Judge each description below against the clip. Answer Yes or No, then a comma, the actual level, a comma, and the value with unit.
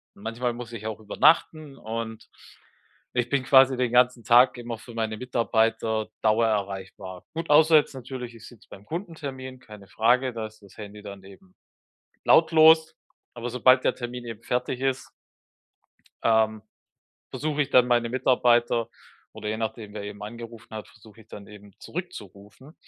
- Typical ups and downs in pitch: Yes, average, 3.0 semitones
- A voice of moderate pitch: No, low, 115 Hz